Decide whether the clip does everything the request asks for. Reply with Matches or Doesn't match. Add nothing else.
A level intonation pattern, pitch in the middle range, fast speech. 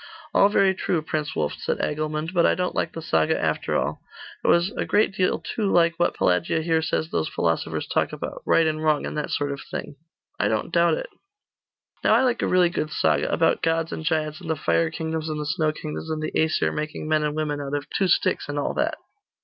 Matches